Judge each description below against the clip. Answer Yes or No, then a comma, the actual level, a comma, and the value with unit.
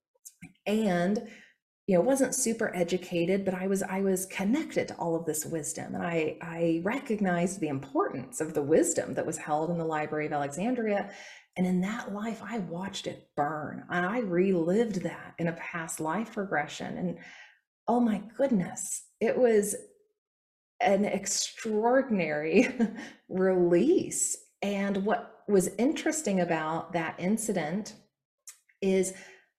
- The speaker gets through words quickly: No, average, 140 wpm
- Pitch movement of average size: Yes, average, 4.8 semitones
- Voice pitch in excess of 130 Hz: Yes, high, 190 Hz